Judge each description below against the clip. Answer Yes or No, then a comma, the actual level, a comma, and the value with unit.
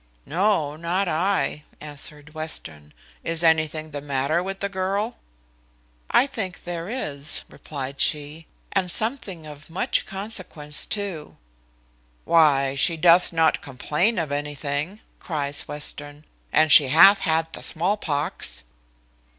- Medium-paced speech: No, slow, 125 wpm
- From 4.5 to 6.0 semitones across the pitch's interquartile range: No, average, 4.1 semitones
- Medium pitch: Yes, medium, 160 Hz